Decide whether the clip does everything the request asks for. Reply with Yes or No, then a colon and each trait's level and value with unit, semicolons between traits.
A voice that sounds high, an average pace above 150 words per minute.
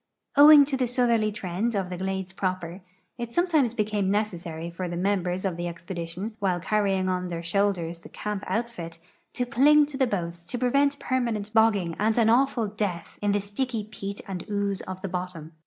Yes: high, 200 Hz; average, 190 wpm